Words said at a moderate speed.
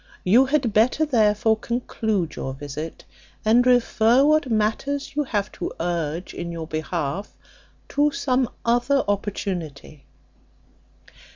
No: slow, 115 wpm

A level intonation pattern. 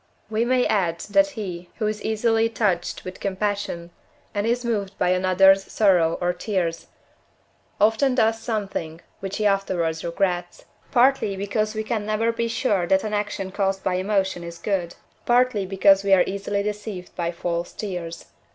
No: average, 3.2 semitones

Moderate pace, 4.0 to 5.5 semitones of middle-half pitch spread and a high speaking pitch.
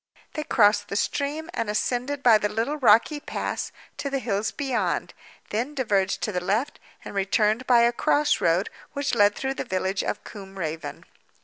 Yes: average, 180 wpm; average, 5.2 semitones; high, 225 Hz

